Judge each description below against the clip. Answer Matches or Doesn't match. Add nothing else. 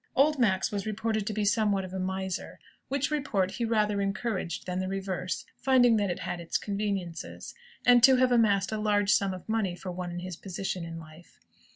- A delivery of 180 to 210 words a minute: Matches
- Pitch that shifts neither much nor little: Matches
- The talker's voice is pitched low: Doesn't match